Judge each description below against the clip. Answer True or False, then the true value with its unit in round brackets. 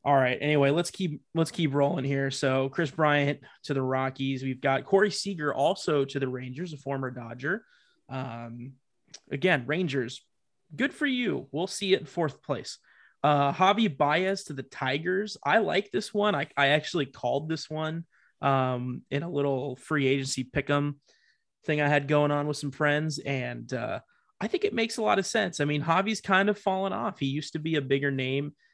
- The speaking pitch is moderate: True (145 Hz)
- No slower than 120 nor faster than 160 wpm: False (195 wpm)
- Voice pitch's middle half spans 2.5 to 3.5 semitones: False (5.1 semitones)